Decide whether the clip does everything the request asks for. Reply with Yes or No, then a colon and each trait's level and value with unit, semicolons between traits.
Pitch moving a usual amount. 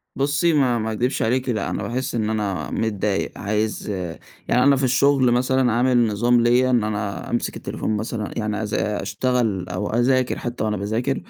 Yes: average, 3.1 semitones